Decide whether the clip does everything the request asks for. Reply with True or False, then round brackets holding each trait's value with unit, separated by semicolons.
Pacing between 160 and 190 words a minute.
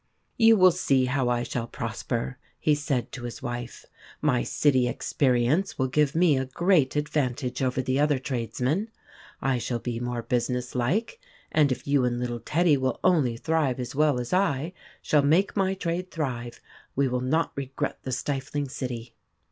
True (180 wpm)